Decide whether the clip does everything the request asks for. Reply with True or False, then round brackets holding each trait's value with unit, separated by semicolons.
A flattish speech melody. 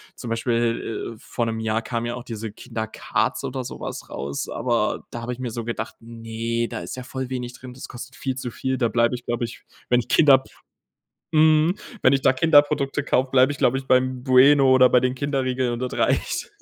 True (2.1 semitones)